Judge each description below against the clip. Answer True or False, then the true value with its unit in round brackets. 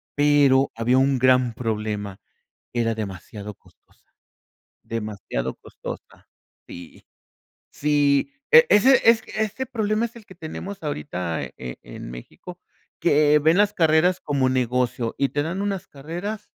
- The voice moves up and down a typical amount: False (8.1 semitones)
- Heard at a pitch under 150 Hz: True (140 Hz)